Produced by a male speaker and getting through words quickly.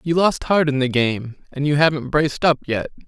Yes: male; fast, 235 wpm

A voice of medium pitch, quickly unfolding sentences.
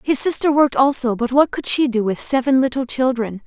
No: very high, 255 Hz; fast, 225 wpm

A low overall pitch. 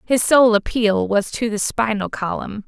No: high, 215 Hz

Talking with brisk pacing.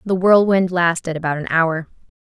No: average, 160 wpm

